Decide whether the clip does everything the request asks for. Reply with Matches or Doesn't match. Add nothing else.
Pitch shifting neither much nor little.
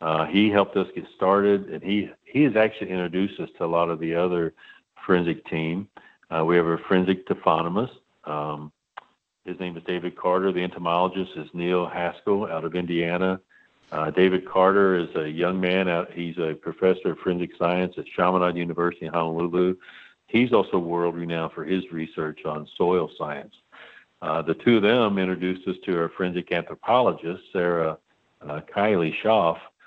Doesn't match